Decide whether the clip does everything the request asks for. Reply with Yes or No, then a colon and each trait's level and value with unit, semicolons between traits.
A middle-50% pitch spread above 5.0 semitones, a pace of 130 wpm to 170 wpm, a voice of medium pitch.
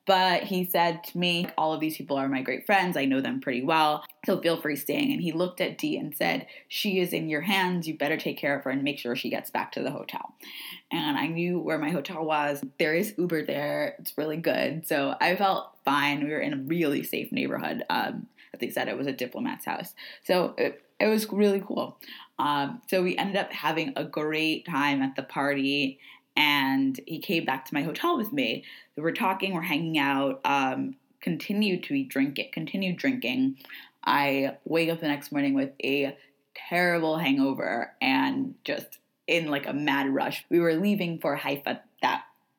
No: wide, 5.4 semitones; fast, 205 wpm; medium, 160 Hz